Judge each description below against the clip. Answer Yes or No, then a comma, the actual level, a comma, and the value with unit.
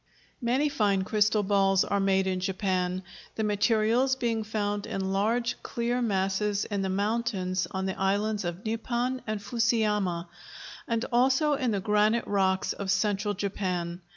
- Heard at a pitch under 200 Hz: No, high, 205 Hz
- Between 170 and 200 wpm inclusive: No, average, 150 wpm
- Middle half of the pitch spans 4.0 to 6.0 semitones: No, average, 3.0 semitones